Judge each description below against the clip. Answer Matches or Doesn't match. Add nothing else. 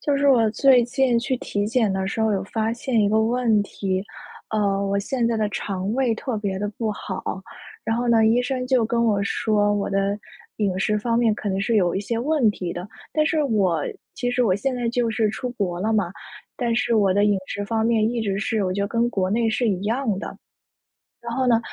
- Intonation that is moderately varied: Matches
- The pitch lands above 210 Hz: Matches